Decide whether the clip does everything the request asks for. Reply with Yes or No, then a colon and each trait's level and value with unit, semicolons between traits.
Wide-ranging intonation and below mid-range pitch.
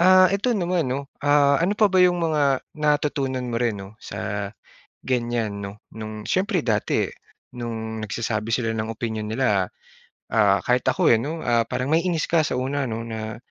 Yes: wide, 6.1 semitones; low, 125 Hz